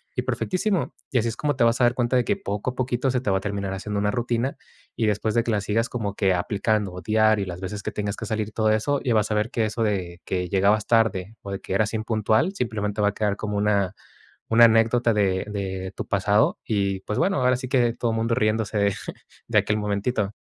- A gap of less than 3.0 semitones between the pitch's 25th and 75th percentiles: Yes, narrow, 2.5 semitones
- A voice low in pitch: Yes, low, 110 Hz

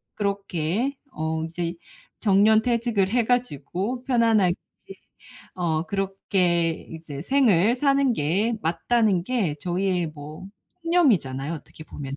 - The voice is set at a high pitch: Yes, high, 195 Hz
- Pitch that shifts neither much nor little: No, wide, 6.2 semitones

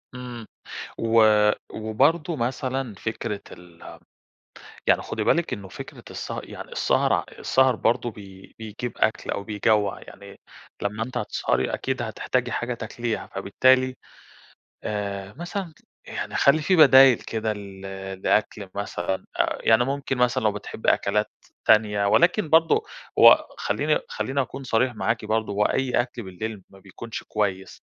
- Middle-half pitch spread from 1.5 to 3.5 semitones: No, average, 4.1 semitones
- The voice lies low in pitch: Yes, low, 110 Hz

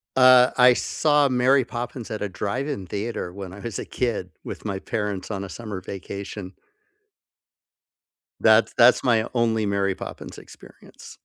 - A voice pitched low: Yes, low, 110 Hz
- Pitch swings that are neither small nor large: Yes, average, 4.0 semitones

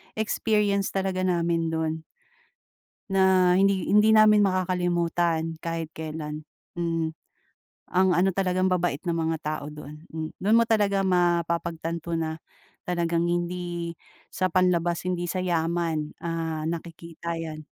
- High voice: No, medium, 170 Hz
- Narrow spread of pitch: Yes, narrow, 2.2 semitones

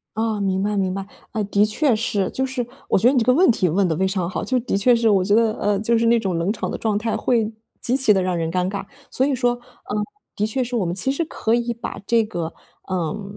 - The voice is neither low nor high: No, high, 215 Hz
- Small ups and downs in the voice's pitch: No, average, 3.7 semitones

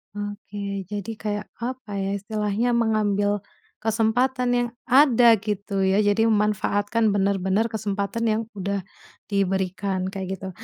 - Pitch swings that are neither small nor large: No, narrow, 2.1 semitones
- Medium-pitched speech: No, high, 205 Hz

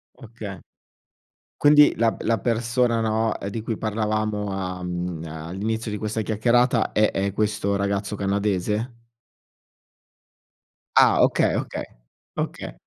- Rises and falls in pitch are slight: Yes, narrow, 2.3 semitones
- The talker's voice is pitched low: Yes, low, 105 Hz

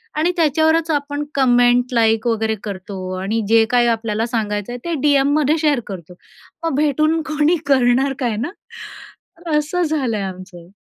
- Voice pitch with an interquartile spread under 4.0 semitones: No, average, 5.2 semitones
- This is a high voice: Yes, high, 245 Hz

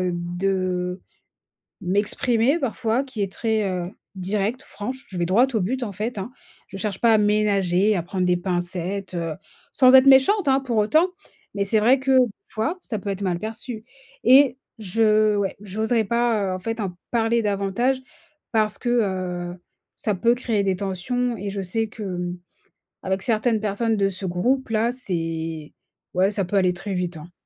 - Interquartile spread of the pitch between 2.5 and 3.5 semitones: No, average, 4.1 semitones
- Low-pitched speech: No, high, 205 Hz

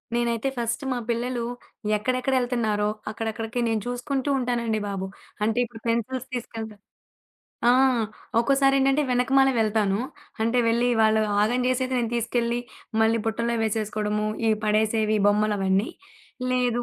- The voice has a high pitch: Yes, high, 230 Hz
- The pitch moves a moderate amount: No, narrow, 2.2 semitones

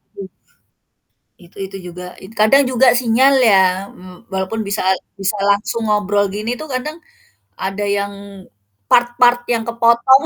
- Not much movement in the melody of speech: No, average, 3.4 semitones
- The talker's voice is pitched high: Yes, high, 215 Hz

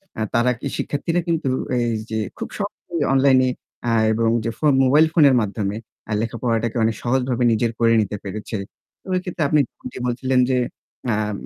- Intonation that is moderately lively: Yes, average, 3.8 semitones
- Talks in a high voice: No, low, 125 Hz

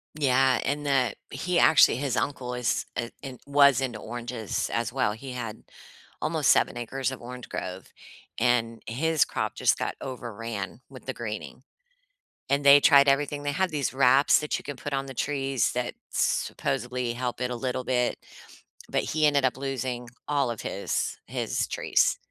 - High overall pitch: No, low, 130 Hz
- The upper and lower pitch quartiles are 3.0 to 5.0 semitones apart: No, narrow, 2.6 semitones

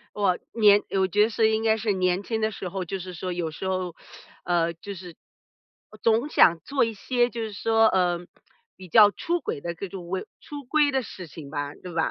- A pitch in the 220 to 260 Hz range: No, high, 195 Hz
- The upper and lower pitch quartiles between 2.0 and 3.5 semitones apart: No, average, 4.0 semitones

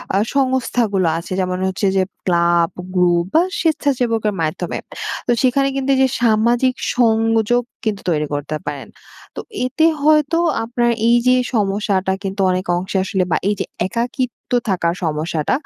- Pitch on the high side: Yes, high, 215 Hz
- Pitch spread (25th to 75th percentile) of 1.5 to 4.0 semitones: No, average, 5.3 semitones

